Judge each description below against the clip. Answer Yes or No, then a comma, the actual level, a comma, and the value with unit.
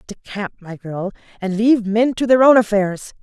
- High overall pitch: Yes, high, 210 Hz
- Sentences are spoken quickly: No, average, 185 wpm